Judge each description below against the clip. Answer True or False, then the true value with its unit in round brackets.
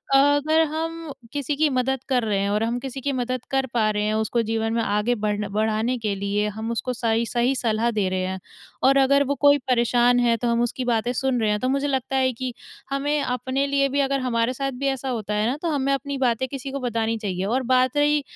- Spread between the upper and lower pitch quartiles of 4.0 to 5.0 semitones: False (3.5 semitones)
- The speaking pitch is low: False (250 Hz)